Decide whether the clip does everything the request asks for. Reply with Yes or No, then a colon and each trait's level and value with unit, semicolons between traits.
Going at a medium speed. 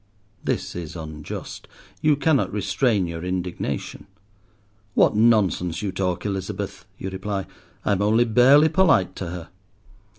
No: slow, 130 wpm